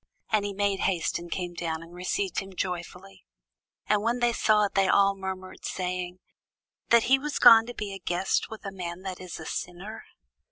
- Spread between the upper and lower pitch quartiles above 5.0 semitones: No, average, 2.9 semitones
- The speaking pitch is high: Yes, high, 195 Hz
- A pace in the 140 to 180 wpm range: No, average, 195 wpm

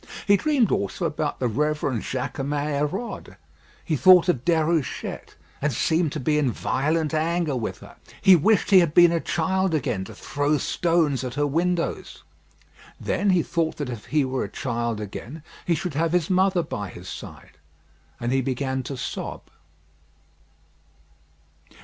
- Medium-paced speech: Yes, average, 160 wpm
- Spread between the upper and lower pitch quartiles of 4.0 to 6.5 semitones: Yes, average, 4.6 semitones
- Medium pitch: Yes, medium, 150 Hz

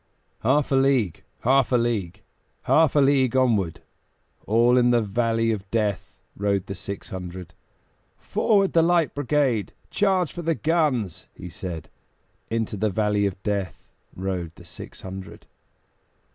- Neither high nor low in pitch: No, low, 115 Hz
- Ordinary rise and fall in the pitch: No, wide, 5.8 semitones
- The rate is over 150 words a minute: No, average, 145 wpm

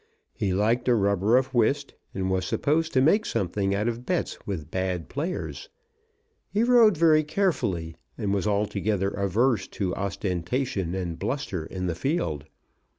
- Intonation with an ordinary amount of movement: No, wide, 6.7 semitones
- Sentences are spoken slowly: No, average, 150 wpm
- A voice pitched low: Yes, low, 105 Hz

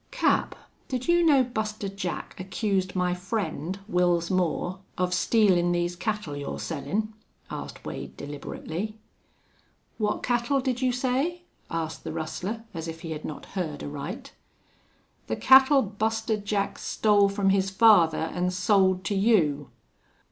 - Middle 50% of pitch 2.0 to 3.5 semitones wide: No, average, 4.3 semitones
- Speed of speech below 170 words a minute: Yes, average, 140 wpm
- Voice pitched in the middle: No, high, 195 Hz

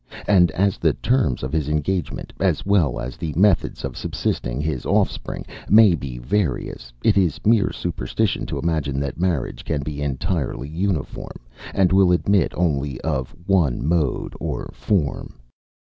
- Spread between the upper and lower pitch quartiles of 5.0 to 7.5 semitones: Yes, wide, 5.5 semitones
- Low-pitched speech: Yes, very low, 80 Hz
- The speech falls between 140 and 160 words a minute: Yes, average, 150 wpm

